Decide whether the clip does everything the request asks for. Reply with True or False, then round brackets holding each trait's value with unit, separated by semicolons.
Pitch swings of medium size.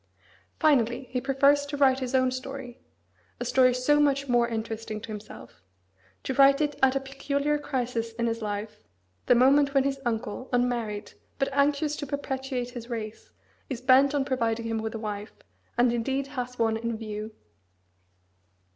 True (3.2 semitones)